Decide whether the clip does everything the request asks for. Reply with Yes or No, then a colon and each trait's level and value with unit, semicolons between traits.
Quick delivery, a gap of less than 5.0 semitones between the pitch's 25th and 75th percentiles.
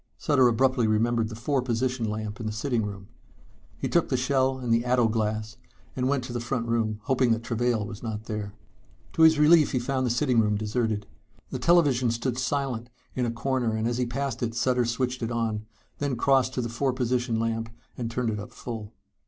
Yes: fast, 215 wpm; narrow, 2.5 semitones